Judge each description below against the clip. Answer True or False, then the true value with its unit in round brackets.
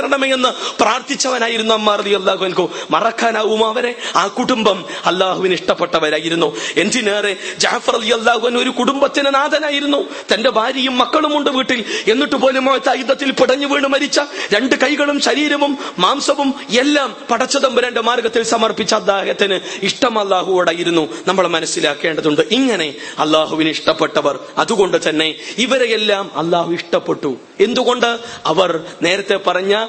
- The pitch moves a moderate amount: False (6.0 semitones)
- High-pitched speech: True (230 Hz)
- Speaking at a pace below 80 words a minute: False (85 wpm)